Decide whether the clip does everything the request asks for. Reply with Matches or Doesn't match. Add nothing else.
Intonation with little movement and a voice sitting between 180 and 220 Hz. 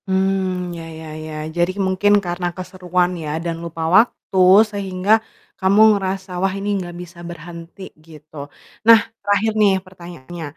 Matches